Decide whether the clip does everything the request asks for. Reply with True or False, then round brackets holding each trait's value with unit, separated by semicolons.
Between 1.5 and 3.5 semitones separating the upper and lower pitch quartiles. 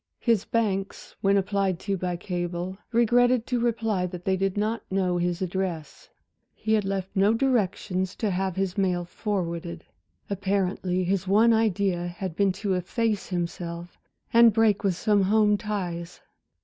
True (2.9 semitones)